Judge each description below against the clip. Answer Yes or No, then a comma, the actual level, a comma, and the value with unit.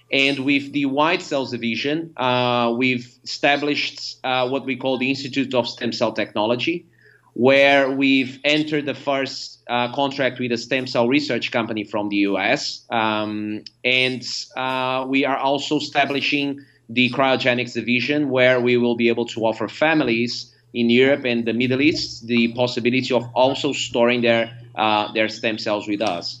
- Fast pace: No, average, 160 wpm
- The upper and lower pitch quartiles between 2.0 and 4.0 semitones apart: Yes, narrow, 2.5 semitones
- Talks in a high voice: No, low, 125 Hz